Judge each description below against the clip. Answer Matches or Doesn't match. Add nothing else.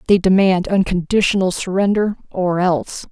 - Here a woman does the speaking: Matches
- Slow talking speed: Matches